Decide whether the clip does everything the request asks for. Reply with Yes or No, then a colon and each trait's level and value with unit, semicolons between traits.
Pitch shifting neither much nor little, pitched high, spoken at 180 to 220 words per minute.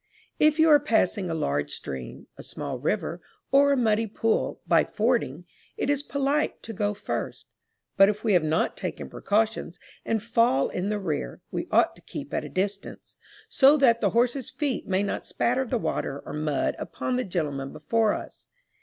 No: wide, 7.1 semitones; high, 210 Hz; average, 185 wpm